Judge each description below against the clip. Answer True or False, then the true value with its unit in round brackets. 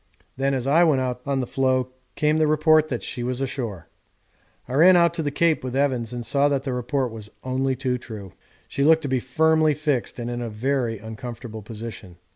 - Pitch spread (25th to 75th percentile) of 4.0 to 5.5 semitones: False (3.3 semitones)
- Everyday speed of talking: False (215 wpm)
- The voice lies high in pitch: False (130 Hz)